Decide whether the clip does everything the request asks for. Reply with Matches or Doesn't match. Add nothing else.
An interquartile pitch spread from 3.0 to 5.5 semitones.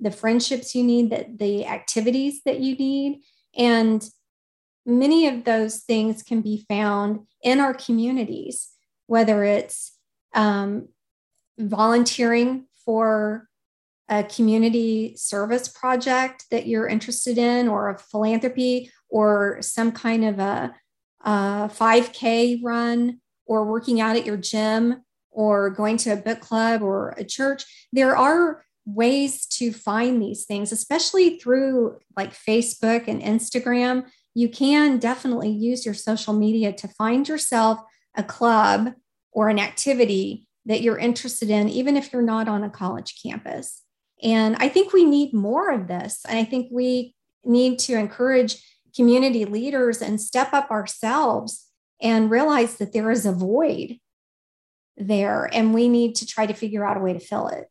Doesn't match